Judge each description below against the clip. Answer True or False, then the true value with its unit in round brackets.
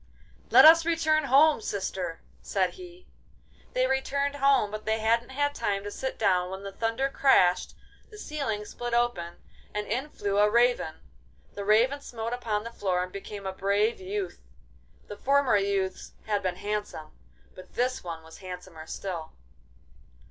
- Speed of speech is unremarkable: True (160 wpm)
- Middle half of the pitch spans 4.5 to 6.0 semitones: True (5.5 semitones)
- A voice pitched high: True (210 Hz)